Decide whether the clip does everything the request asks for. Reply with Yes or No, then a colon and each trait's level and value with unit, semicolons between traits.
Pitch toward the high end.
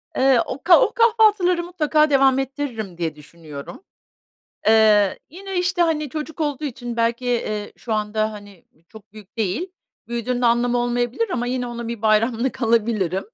Yes: high, 240 Hz